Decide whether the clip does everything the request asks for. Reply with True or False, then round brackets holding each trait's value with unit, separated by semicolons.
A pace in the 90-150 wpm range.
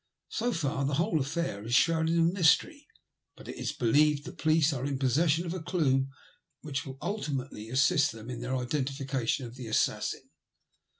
False (175 wpm)